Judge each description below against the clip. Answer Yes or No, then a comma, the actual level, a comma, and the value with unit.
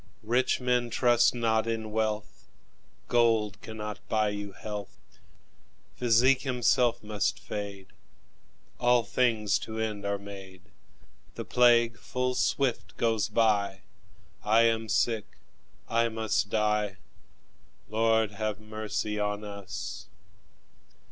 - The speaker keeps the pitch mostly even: Yes, narrow, 2.1 semitones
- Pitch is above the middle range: No, low, 110 Hz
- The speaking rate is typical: No, slow, 110 wpm